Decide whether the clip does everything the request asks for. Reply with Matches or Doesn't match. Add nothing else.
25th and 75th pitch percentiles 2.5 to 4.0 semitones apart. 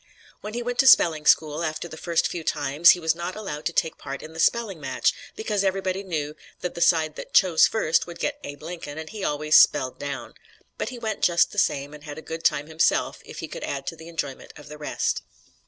Matches